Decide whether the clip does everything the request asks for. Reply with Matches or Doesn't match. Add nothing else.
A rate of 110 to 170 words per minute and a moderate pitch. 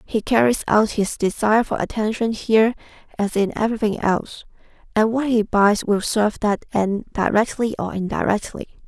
Doesn't match